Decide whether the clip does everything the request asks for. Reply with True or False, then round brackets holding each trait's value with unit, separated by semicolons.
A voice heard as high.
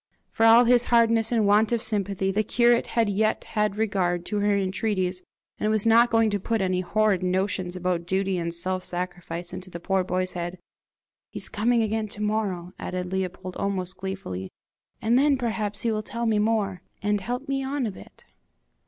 True (205 Hz)